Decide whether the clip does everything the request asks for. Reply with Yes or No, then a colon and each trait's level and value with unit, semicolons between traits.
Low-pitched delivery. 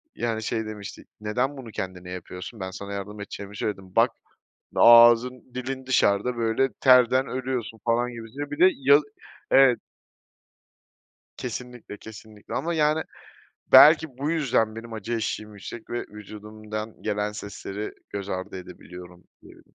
Yes: low, 115 Hz